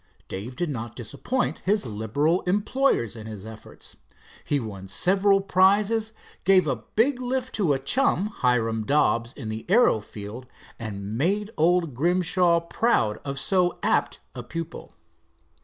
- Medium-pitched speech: Yes, medium, 160 Hz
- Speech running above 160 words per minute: No, average, 140 wpm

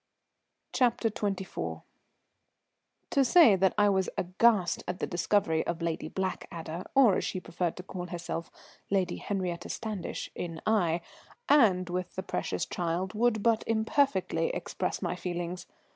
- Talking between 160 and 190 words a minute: No, average, 140 wpm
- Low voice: No, medium, 185 Hz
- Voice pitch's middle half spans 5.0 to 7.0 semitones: No, average, 3.7 semitones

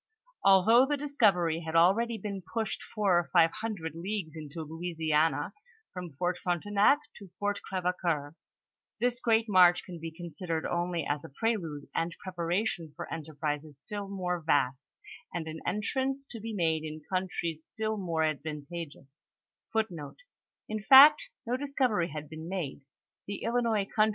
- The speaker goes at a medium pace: No, slow, 120 wpm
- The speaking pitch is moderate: Yes, medium, 175 Hz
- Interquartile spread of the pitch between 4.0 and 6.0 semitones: Yes, average, 4.3 semitones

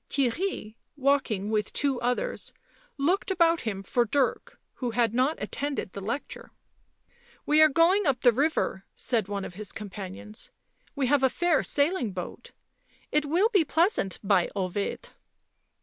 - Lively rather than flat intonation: Yes, wide, 6.7 semitones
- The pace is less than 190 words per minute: Yes, average, 165 wpm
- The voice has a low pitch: No, very high, 260 Hz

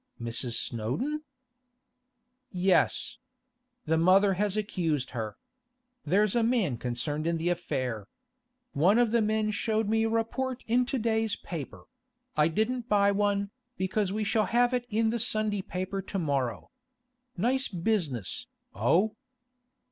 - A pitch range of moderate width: No, wide, 6.1 semitones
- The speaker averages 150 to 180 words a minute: No, slow, 135 wpm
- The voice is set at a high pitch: Yes, high, 200 Hz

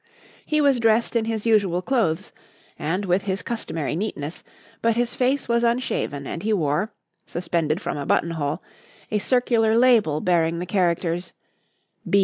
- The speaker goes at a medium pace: Yes, average, 155 wpm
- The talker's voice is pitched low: No, high, 200 Hz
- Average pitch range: No, wide, 5.7 semitones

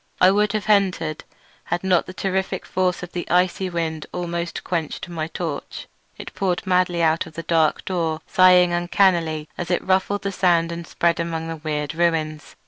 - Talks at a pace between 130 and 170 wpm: No, average, 180 wpm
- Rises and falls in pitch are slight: Yes, narrow, 2.1 semitones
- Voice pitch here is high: No, medium, 175 Hz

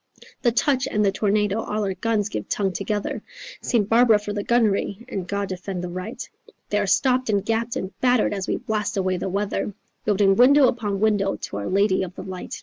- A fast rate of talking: Yes, fast, 210 wpm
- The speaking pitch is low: No, high, 205 Hz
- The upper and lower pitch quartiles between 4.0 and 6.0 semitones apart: No, average, 2.7 semitones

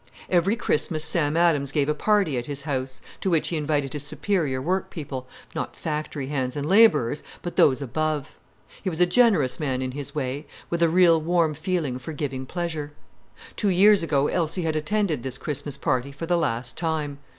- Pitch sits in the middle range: Yes, medium, 150 Hz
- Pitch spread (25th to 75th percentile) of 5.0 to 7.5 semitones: No, average, 3.7 semitones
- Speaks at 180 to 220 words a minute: Yes, average, 185 wpm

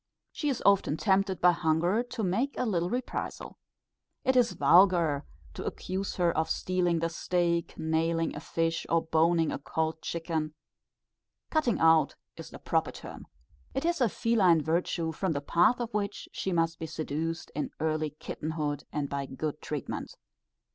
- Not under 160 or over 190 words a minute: Yes, average, 165 wpm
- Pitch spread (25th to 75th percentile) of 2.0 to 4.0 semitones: Yes, average, 3.3 semitones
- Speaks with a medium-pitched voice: Yes, medium, 165 Hz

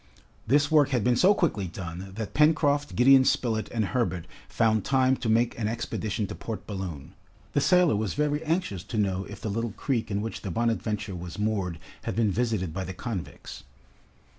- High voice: No, low, 110 Hz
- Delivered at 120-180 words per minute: No, average, 190 wpm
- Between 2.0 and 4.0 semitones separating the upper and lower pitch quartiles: No, average, 5.2 semitones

